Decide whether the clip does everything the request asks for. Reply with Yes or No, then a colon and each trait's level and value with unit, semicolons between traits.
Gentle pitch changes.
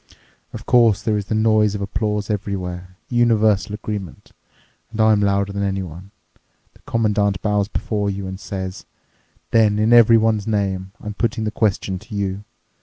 Yes: narrow, 1.8 semitones